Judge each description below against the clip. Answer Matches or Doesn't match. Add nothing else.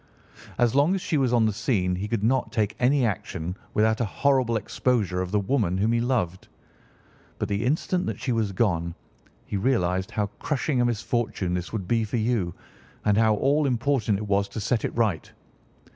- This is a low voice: Matches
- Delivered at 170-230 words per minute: Matches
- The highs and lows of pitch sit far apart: Doesn't match